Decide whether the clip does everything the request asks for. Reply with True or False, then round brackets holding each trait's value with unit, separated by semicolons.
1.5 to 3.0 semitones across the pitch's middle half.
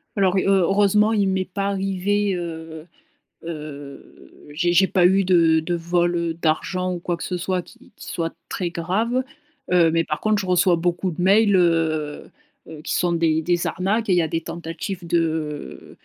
True (2.6 semitones)